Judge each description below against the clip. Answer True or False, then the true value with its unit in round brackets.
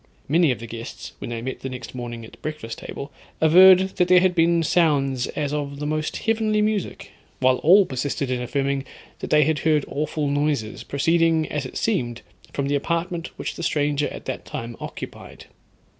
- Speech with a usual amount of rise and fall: True (4.1 semitones)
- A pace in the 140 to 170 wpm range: False (190 wpm)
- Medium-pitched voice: True (150 Hz)